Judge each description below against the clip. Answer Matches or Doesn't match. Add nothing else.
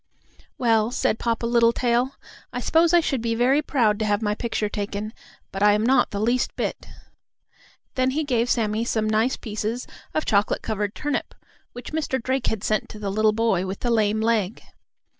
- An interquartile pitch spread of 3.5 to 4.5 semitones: Doesn't match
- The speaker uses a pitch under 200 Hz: Doesn't match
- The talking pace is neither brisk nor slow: Matches